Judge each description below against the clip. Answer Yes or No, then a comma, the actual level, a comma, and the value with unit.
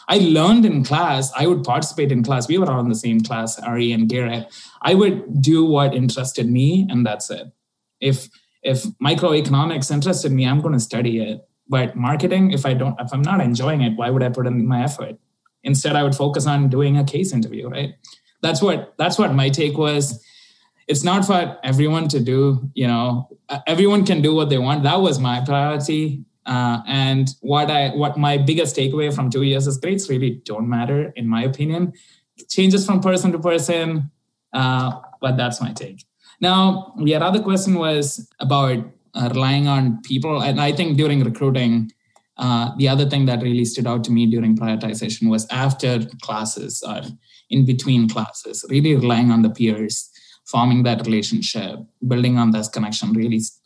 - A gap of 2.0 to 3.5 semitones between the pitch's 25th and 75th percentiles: No, average, 3.9 semitones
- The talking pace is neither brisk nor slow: Yes, average, 190 wpm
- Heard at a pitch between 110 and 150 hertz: Yes, low, 135 Hz